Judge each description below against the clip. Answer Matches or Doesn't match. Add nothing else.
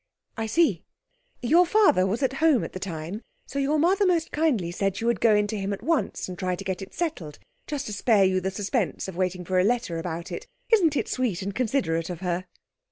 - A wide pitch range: Matches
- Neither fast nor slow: Doesn't match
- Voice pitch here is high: Matches